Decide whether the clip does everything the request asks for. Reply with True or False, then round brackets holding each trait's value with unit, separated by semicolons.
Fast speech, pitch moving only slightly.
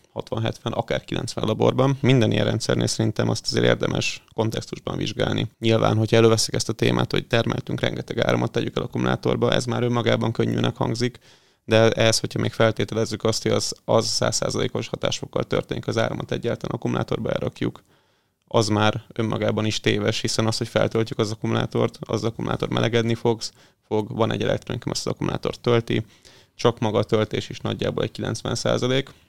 True (160 wpm; 1.8 semitones)